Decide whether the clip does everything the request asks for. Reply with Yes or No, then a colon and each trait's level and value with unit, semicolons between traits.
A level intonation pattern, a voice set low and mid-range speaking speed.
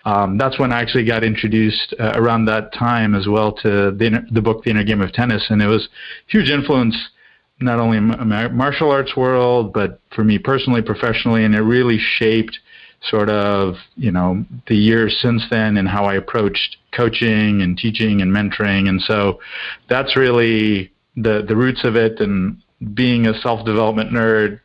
Yes: narrow, 2.2 semitones; low, 110 Hz; average, 185 wpm